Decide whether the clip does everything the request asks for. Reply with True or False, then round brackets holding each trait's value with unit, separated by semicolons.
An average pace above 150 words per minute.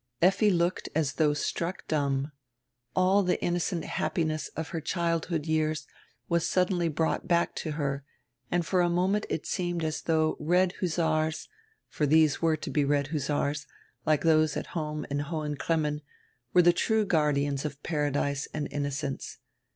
True (165 wpm)